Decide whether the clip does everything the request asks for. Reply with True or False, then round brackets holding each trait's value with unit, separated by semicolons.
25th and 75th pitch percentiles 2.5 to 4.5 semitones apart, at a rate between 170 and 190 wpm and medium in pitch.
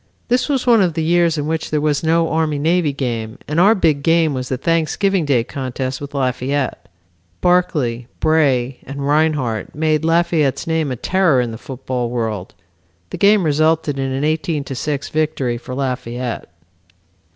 True (4.0 semitones; 175 wpm; 145 Hz)